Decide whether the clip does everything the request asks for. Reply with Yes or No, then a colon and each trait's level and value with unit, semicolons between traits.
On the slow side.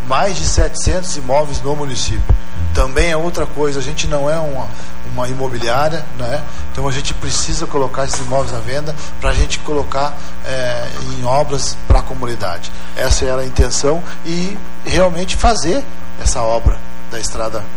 No: average, 160 wpm